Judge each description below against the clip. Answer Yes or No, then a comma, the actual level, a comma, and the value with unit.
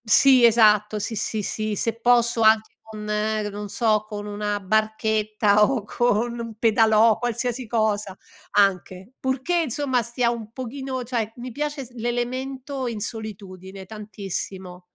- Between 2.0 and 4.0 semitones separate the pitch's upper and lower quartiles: Yes, narrow, 2.5 semitones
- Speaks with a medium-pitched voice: No, high, 220 Hz